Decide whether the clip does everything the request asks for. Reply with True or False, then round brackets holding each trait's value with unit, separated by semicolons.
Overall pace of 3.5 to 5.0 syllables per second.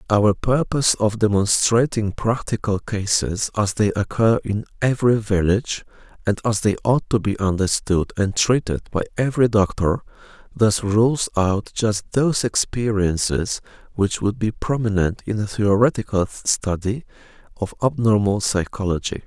True (4.7 syllables/s)